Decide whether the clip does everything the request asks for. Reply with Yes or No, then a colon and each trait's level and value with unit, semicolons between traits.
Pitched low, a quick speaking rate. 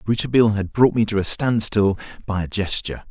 No: low, 105 Hz; average, 195 wpm